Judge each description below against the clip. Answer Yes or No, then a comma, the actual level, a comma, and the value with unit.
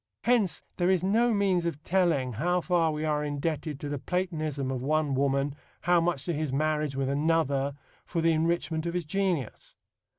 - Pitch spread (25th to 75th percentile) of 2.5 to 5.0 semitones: Yes, average, 3.6 semitones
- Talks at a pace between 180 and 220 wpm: Yes, average, 185 wpm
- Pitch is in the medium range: Yes, medium, 155 Hz